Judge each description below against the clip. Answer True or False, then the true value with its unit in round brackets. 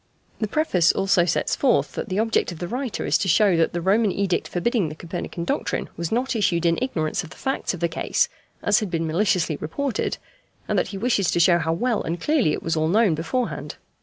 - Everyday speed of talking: False (225 wpm)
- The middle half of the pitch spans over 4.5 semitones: True (5.2 semitones)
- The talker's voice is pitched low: False (185 Hz)